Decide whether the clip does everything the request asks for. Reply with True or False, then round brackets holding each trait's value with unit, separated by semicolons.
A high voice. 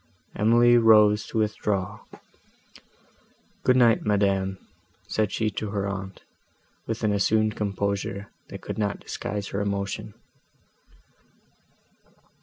False (105 Hz)